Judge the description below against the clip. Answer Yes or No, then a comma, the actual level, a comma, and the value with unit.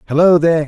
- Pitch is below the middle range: No, medium, 160 Hz